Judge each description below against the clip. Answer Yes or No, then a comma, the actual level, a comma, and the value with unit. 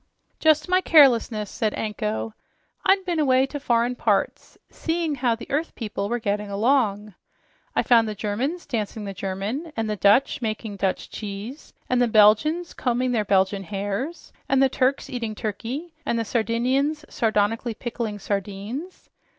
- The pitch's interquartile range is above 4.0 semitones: Yes, average, 4.5 semitones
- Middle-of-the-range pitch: No, high, 230 Hz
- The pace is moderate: Yes, average, 155 wpm